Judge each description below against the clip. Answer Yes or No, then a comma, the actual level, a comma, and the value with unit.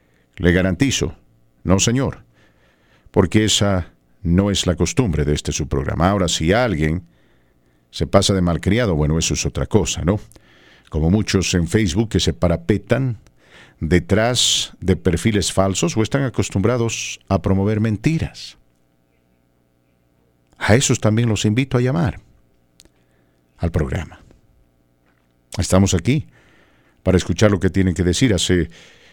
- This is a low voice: Yes, very low, 90 Hz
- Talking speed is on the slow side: Yes, slow, 130 wpm